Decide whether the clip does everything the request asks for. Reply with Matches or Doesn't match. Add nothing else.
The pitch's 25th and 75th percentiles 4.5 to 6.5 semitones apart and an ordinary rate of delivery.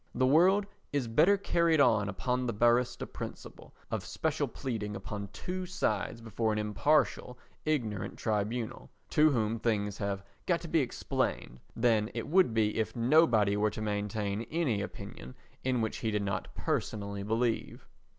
Matches